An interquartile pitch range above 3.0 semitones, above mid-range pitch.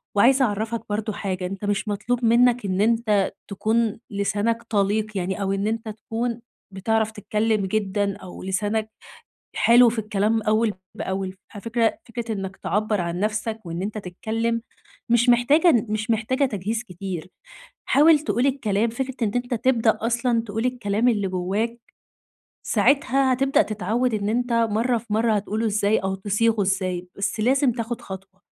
No: average, 2.7 semitones; high, 220 Hz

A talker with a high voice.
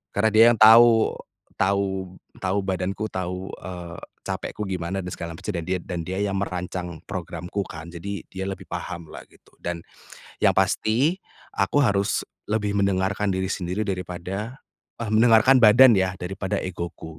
No: very low, 95 Hz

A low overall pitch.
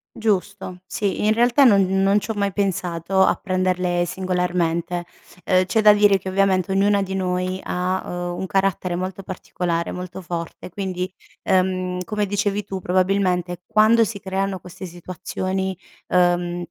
No: medium, 185 Hz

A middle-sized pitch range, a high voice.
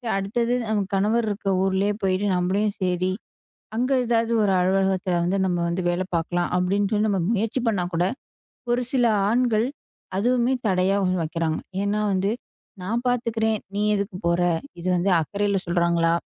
Yes: average, 3.4 semitones; high, 195 Hz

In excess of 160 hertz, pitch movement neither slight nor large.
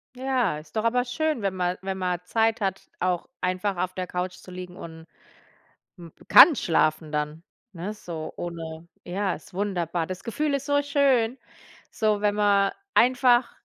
Yes: high, 190 Hz; average, 4.9 semitones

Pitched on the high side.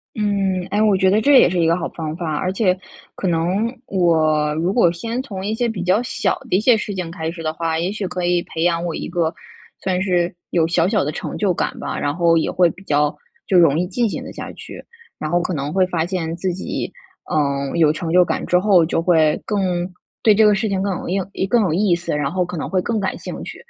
No: medium, 180 Hz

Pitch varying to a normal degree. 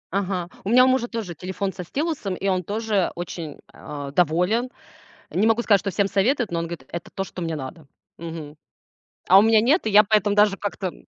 Yes: average, 4.1 semitones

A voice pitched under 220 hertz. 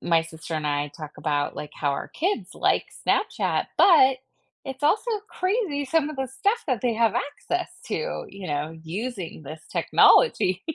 No: high, 235 Hz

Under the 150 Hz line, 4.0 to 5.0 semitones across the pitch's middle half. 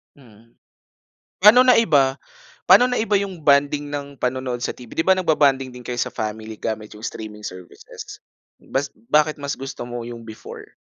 Yes: low, 135 Hz; average, 4.6 semitones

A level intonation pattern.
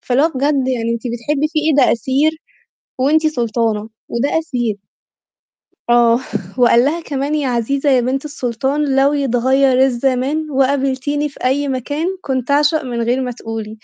No: average, 3.1 semitones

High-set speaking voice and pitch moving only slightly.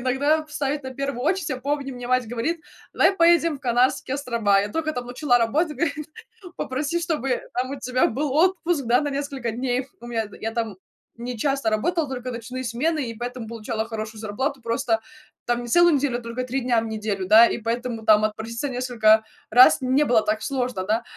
No: very high, 250 Hz; average, 3.7 semitones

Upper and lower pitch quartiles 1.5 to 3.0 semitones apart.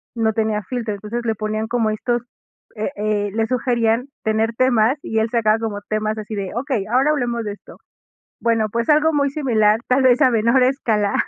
Yes: narrow, 2.6 semitones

